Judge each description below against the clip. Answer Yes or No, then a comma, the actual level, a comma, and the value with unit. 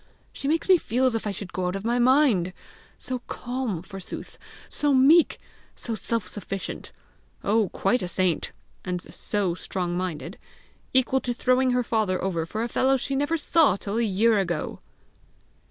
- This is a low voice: No, high, 220 Hz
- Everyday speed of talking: Yes, average, 170 wpm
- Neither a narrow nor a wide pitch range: No, wide, 5.7 semitones